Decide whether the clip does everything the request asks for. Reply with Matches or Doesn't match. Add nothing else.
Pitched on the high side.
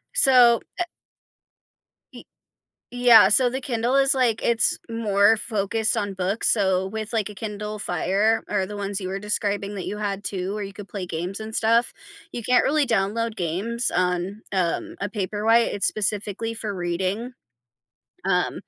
Matches